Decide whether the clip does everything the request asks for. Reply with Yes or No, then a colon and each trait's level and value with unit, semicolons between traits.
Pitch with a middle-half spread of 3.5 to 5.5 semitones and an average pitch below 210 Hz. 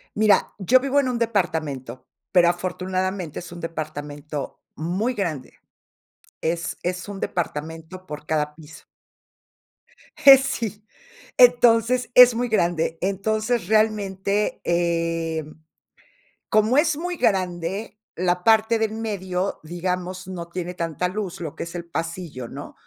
Yes: average, 4.5 semitones; medium, 185 Hz